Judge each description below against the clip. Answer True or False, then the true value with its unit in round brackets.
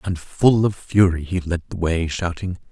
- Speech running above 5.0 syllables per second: False (4.5 syllables/s)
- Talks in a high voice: False (90 Hz)